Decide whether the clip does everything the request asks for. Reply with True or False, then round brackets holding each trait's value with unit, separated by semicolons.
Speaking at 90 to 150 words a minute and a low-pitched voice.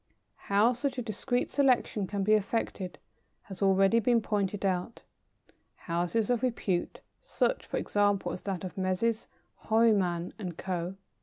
False (140 wpm; 205 Hz)